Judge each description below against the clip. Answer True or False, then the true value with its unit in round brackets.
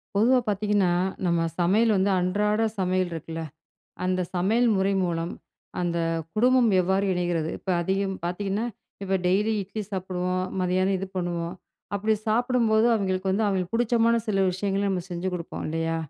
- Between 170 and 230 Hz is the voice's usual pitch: True (190 Hz)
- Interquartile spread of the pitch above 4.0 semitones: False (2.8 semitones)